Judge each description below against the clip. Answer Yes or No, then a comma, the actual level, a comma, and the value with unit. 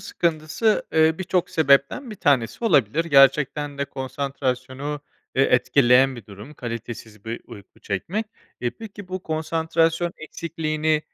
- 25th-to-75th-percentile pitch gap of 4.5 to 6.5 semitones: No, average, 4.1 semitones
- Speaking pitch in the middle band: Yes, medium, 145 Hz